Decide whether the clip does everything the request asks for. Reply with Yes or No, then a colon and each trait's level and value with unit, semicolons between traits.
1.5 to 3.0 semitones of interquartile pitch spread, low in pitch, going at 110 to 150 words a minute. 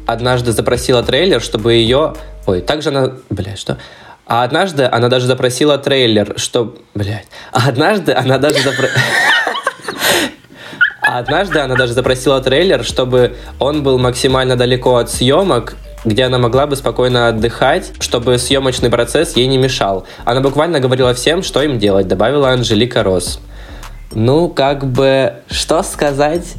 Yes: narrow, 2.5 semitones; low, 130 Hz; average, 140 wpm